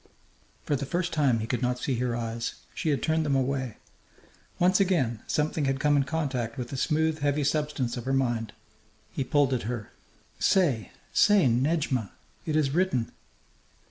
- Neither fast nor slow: Yes, average, 175 wpm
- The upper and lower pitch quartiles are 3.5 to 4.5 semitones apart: Yes, average, 3.9 semitones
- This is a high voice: No, low, 135 Hz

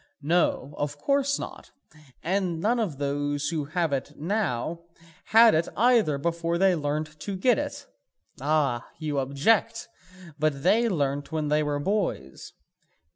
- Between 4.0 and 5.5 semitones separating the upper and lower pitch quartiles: Yes, average, 5.0 semitones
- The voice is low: No, medium, 155 Hz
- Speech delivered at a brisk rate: No, average, 140 wpm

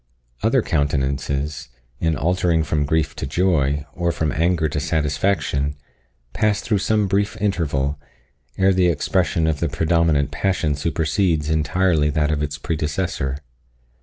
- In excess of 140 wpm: No, slow, 135 wpm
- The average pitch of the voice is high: No, very low, 80 Hz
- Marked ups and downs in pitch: No, average, 3.7 semitones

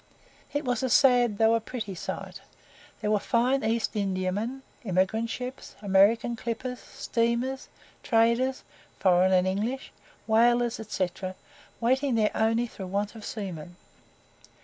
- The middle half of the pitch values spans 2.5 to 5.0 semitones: Yes, average, 3.4 semitones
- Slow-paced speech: Yes, slow, 125 wpm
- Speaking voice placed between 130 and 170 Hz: No, high, 225 Hz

